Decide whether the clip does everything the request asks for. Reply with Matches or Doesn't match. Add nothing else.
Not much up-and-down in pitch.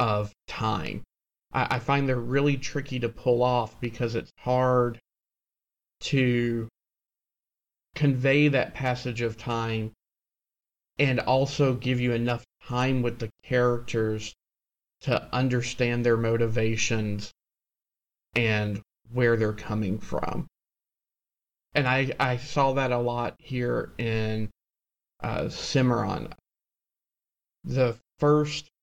Matches